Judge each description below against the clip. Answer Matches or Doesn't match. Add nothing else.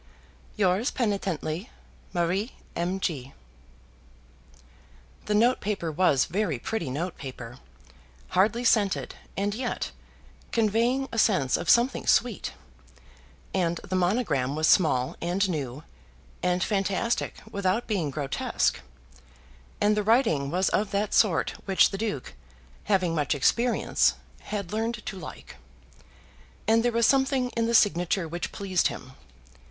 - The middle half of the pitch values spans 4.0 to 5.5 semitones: Matches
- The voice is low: Doesn't match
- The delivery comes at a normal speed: Doesn't match